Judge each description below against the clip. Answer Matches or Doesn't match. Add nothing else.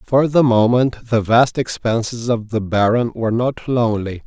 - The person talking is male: Matches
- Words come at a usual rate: Matches